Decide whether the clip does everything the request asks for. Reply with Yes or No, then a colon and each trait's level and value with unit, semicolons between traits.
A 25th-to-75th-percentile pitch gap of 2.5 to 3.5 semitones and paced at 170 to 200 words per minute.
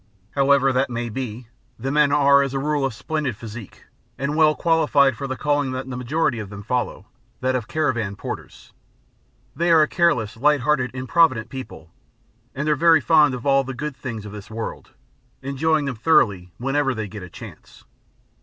No: average, 3.9 semitones; average, 185 wpm